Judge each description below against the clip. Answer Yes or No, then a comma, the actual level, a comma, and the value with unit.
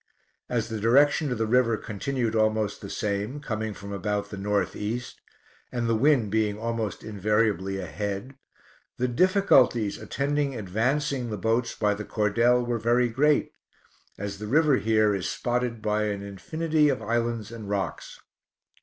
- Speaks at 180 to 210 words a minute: No, average, 155 wpm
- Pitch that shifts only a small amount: No, average, 3.1 semitones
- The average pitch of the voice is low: Yes, low, 110 Hz